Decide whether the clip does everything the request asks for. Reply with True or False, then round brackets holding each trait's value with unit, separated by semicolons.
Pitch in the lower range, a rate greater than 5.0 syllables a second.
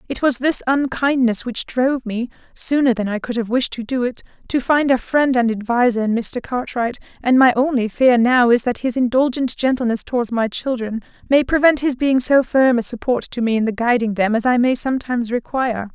False (245 Hz; 5.4 syllables/s)